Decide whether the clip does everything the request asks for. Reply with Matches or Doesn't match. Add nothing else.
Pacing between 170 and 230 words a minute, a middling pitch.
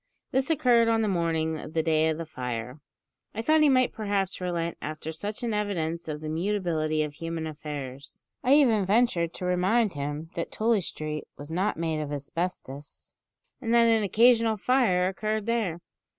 Matches